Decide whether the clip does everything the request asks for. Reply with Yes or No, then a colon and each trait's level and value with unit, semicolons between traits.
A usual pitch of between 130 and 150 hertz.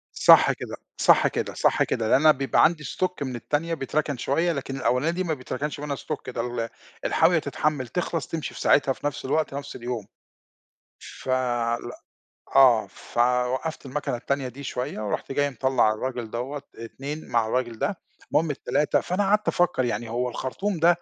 Yes: low, 135 Hz